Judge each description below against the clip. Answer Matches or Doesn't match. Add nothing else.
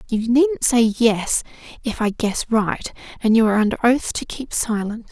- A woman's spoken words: Matches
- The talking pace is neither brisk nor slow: Matches